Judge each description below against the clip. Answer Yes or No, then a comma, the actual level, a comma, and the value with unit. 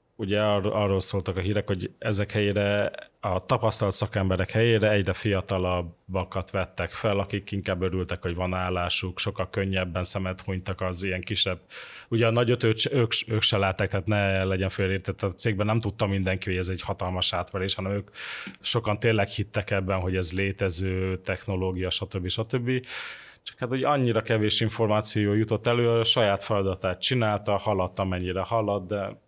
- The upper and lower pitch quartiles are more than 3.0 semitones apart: No, narrow, 2.5 semitones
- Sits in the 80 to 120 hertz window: Yes, low, 100 Hz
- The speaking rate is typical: No, fast, 160 wpm